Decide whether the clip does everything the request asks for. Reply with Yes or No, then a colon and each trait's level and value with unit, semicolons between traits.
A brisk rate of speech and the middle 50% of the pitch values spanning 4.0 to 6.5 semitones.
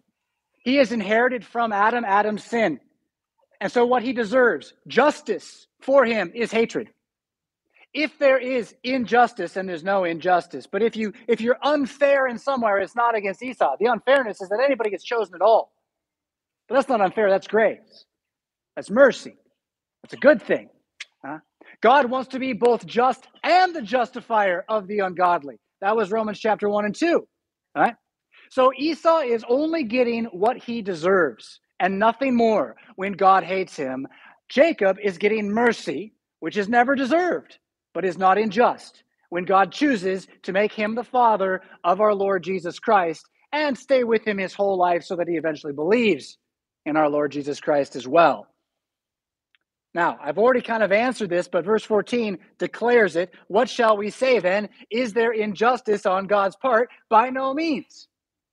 No: average, 165 wpm; average, 4.7 semitones